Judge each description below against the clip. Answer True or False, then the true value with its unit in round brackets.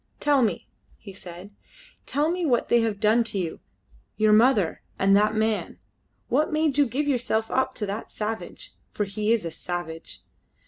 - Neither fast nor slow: True (175 wpm)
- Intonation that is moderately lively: True (4.3 semitones)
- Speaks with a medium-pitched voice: False (220 Hz)